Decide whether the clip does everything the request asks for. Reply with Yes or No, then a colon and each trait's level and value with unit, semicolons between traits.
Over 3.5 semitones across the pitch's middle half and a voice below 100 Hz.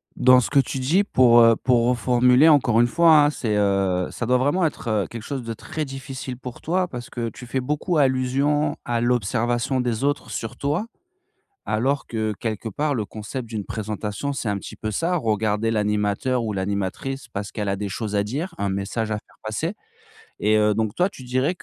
No: average, 4.1 semitones; low, 120 Hz